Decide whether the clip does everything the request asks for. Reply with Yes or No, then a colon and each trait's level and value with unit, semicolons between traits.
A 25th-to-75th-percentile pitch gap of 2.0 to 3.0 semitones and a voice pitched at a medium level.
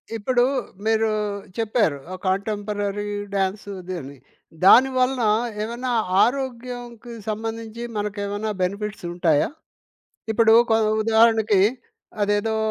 No: narrow, 2.4 semitones; high, 220 Hz